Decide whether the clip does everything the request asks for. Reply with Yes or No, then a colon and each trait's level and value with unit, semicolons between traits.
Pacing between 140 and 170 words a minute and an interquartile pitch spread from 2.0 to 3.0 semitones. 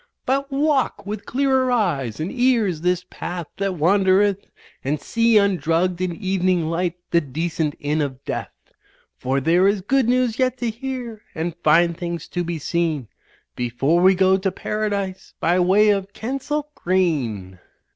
No: average, 155 wpm; average, 4.7 semitones